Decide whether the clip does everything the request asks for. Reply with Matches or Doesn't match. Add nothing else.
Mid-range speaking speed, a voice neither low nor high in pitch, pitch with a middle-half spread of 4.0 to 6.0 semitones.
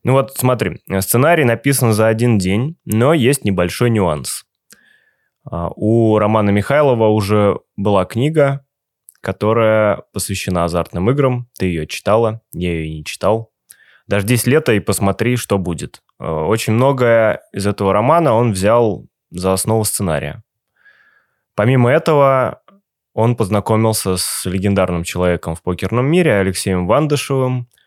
Doesn't match